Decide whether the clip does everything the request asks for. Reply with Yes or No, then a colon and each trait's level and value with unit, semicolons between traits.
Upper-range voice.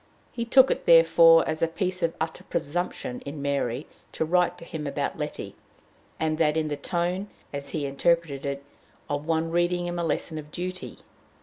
No: medium, 165 Hz